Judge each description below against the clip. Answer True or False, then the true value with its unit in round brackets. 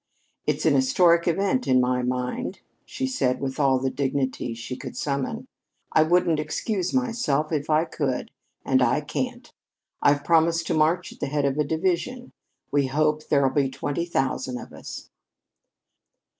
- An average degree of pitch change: True (4.2 semitones)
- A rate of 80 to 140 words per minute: False (160 wpm)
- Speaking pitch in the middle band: True (150 Hz)